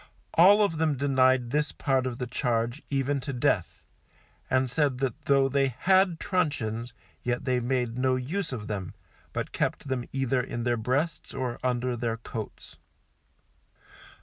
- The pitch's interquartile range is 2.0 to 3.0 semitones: Yes, average, 2.7 semitones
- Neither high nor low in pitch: No, low, 130 Hz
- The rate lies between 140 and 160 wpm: Yes, average, 155 wpm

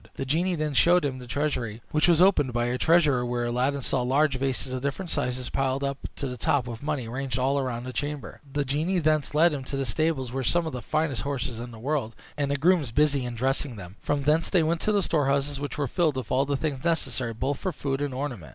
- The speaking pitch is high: No, medium, 140 Hz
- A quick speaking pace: Yes, fast, 250 wpm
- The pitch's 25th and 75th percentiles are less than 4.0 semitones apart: Yes, average, 3.2 semitones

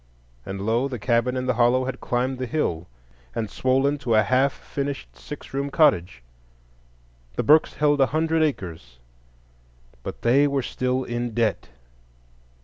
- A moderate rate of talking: Yes, average, 150 wpm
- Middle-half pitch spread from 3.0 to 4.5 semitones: Yes, average, 3.9 semitones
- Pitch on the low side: Yes, low, 125 Hz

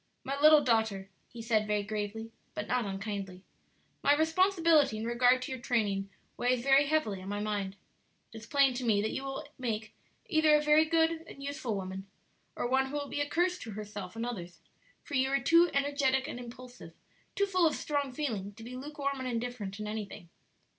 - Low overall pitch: No, high, 245 Hz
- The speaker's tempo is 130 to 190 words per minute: No, average, 200 wpm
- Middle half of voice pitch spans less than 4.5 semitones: No, average, 5.3 semitones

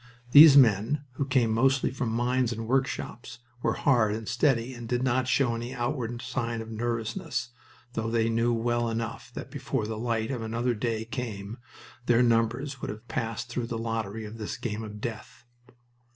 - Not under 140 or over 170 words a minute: No, average, 180 wpm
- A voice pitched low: Yes, low, 115 Hz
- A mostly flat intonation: Yes, narrow, 1.9 semitones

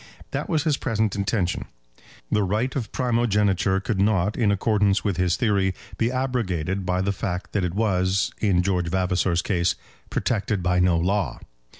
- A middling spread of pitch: Yes, average, 3.0 semitones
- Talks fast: No, average, 165 wpm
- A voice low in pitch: Yes, low, 100 Hz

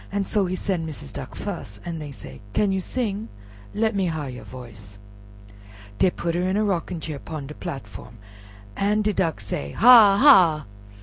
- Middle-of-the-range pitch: Yes, medium, 175 Hz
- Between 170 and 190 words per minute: Yes, average, 180 wpm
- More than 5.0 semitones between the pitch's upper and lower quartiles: Yes, wide, 5.6 semitones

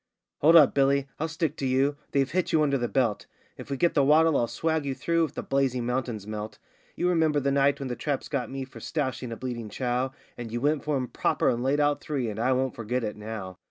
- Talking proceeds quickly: Yes, fast, 250 wpm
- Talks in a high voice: No, low, 135 Hz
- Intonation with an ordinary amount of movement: Yes, average, 3.3 semitones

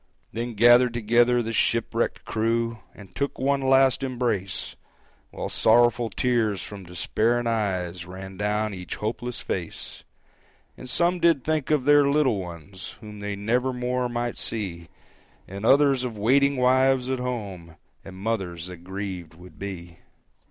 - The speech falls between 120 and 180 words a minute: Yes, average, 145 wpm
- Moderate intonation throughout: Yes, average, 4.7 semitones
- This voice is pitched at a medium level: No, low, 115 Hz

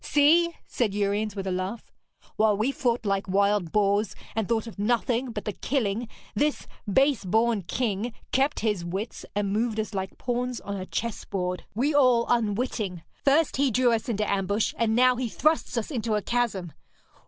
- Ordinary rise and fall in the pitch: Yes, average, 3.5 semitones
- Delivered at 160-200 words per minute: Yes, average, 175 wpm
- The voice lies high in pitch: Yes, high, 220 Hz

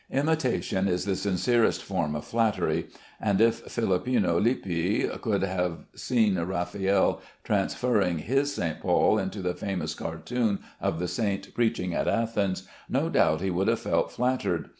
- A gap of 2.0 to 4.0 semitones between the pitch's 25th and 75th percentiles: No, average, 4.4 semitones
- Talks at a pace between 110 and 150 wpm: Yes, average, 145 wpm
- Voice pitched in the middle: No, low, 100 Hz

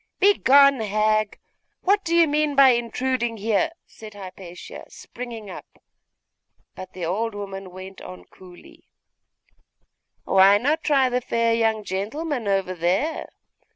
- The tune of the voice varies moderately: No, wide, 5.7 semitones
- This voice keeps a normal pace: No, slow, 125 wpm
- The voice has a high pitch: Yes, high, 220 Hz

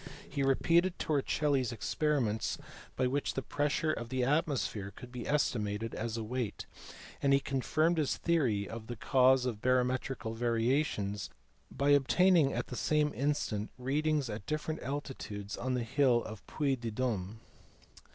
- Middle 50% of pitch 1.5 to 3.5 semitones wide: No, average, 4.1 semitones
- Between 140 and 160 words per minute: Yes, average, 155 wpm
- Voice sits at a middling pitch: No, low, 130 Hz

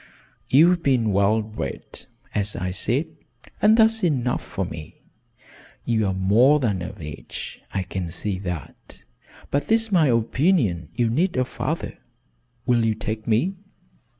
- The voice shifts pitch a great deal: Yes, wide, 7.3 semitones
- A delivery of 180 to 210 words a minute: No, average, 140 wpm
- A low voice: Yes, low, 115 Hz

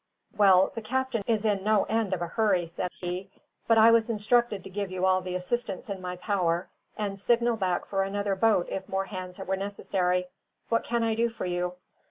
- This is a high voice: Yes, high, 195 Hz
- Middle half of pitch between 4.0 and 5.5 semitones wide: No, average, 3.3 semitones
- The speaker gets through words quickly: Yes, fast, 210 wpm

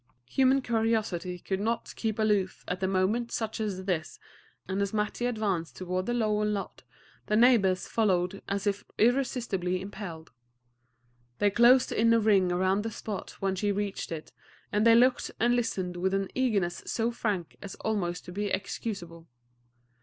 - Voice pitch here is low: No, high, 205 Hz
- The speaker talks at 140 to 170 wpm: Yes, average, 160 wpm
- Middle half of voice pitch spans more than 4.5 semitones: No, average, 3.3 semitones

